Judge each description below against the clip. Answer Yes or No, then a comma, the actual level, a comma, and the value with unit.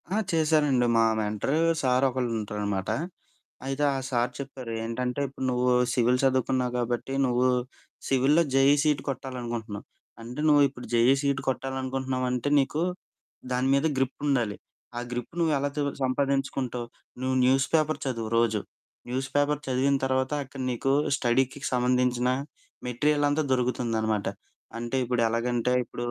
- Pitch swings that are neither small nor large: No, narrow, 2.0 semitones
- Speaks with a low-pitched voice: Yes, low, 130 Hz